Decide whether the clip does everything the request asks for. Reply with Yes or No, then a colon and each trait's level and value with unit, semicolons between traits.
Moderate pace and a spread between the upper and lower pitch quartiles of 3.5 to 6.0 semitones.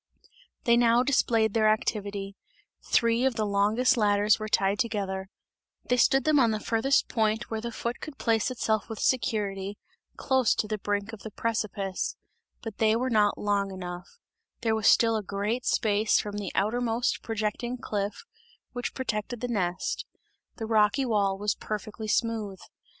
No: average, 160 wpm; narrow, 2.4 semitones